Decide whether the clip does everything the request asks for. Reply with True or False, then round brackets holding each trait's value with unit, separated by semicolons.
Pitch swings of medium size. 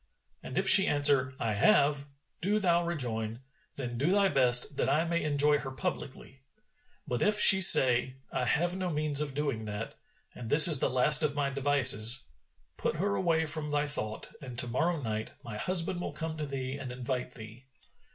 True (4.4 semitones)